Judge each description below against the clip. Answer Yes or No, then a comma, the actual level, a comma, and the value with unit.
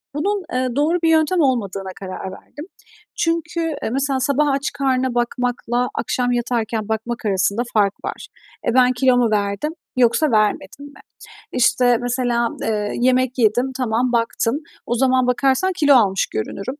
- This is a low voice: No, very high, 250 Hz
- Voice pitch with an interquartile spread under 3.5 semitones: Yes, average, 3.1 semitones